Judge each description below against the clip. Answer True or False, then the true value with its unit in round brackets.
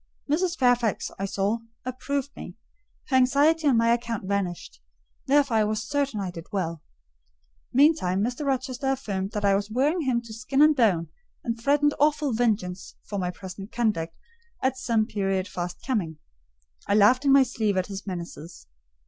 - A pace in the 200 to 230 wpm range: False (165 wpm)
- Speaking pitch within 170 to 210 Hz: False (230 Hz)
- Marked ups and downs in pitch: True (5.7 semitones)